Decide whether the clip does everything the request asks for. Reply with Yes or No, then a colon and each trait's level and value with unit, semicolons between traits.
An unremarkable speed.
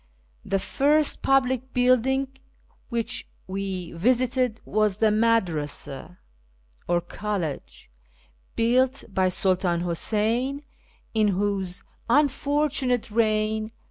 No: slow, 90 wpm